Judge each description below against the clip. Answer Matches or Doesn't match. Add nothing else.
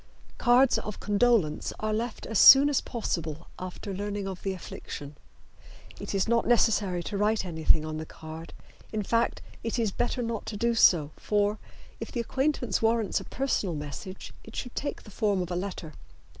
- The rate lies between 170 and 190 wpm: Matches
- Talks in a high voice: Matches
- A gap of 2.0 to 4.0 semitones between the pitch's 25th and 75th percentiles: Doesn't match